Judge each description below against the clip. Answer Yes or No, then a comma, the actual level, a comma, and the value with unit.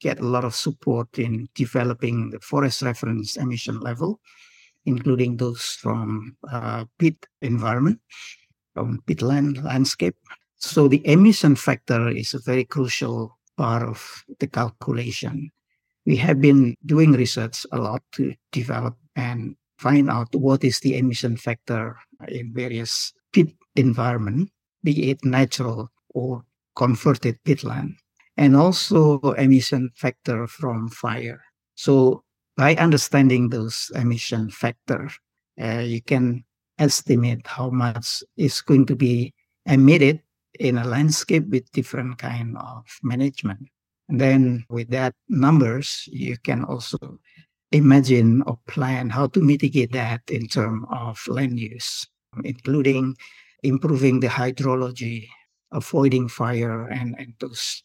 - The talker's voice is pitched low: Yes, low, 130 Hz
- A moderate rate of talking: No, slow, 125 wpm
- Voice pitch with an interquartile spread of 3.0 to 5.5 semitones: No, narrow, 2.6 semitones